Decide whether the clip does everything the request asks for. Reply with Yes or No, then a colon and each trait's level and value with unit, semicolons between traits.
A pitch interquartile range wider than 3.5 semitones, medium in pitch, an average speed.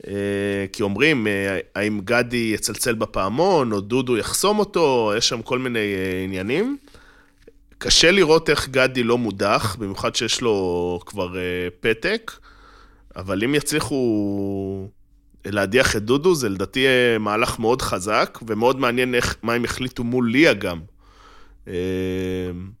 No: average, 4.3 semitones; low, 105 Hz; average, 120 wpm